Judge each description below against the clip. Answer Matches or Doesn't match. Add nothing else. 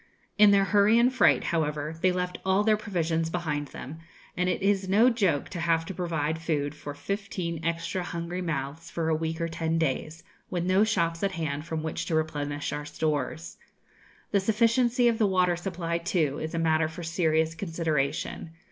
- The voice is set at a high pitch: Doesn't match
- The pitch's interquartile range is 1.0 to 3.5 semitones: Matches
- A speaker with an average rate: Matches